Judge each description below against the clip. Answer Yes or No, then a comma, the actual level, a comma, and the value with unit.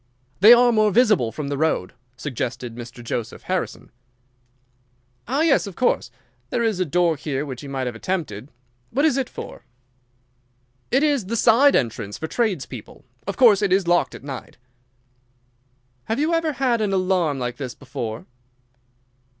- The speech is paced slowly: No, average, 165 wpm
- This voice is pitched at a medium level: Yes, medium, 180 Hz